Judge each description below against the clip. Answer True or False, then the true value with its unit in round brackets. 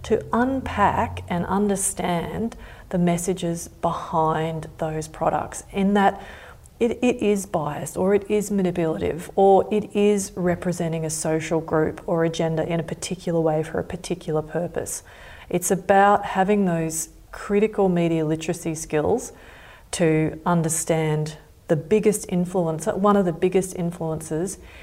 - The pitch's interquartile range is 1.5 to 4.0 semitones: True (3.5 semitones)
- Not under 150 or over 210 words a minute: False (135 wpm)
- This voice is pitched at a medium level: True (175 Hz)